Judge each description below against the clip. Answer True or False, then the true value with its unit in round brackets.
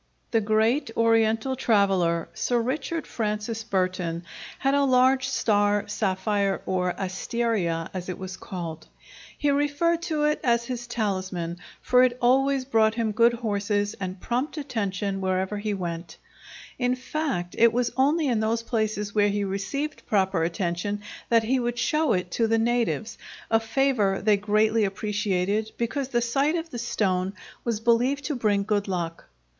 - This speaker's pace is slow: False (155 wpm)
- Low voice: False (220 Hz)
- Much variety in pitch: False (4.1 semitones)